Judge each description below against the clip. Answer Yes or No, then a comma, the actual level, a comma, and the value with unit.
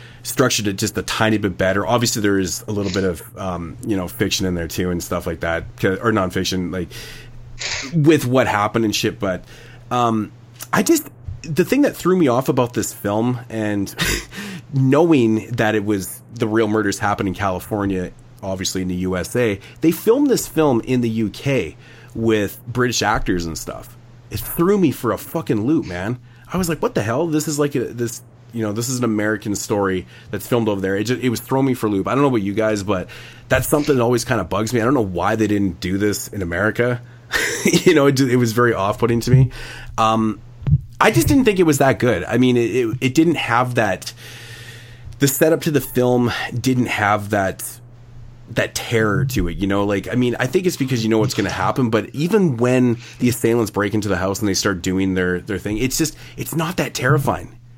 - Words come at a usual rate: No, fast, 220 wpm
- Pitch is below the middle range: Yes, low, 115 Hz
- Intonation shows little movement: No, average, 3.6 semitones